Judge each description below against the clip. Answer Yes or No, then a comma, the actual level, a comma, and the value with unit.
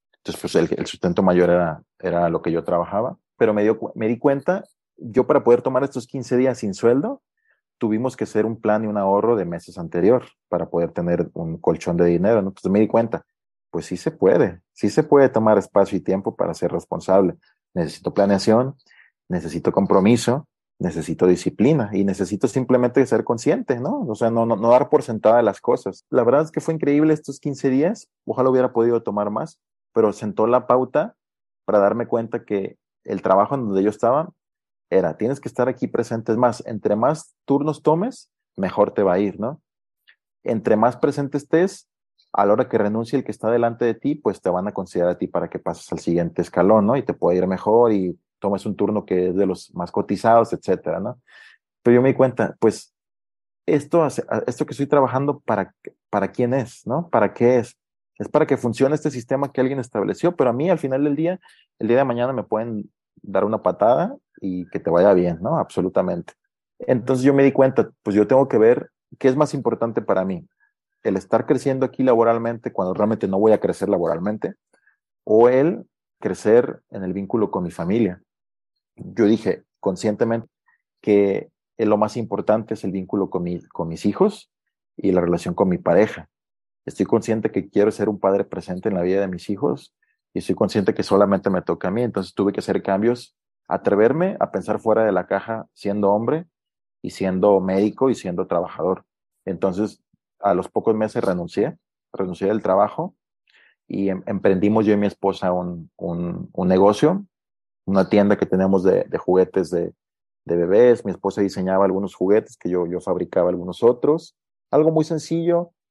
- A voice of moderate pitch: No, low, 110 Hz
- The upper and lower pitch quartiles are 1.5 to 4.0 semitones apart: No, average, 4.9 semitones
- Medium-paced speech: No, fast, 195 wpm